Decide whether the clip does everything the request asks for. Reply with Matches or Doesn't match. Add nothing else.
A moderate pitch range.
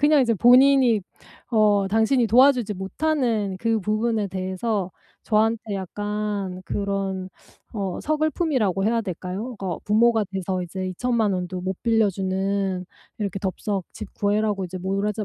Matches